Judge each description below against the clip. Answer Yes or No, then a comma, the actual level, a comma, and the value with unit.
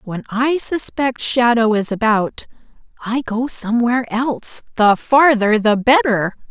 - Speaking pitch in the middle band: No, high, 235 Hz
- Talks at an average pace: No, slow, 130 wpm